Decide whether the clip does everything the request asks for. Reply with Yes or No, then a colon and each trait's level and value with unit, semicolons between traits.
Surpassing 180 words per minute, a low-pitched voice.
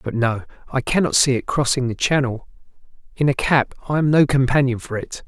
Yes: fast, 205 wpm; low, 130 Hz